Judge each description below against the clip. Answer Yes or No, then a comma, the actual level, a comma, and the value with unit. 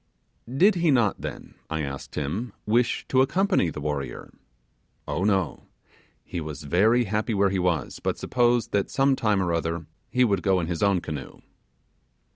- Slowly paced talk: No, average, 170 wpm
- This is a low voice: Yes, low, 100 Hz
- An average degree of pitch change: No, wide, 6.6 semitones